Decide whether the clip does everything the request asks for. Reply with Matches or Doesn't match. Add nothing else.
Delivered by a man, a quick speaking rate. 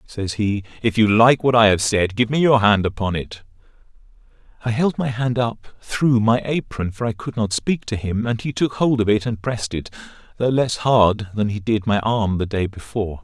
Matches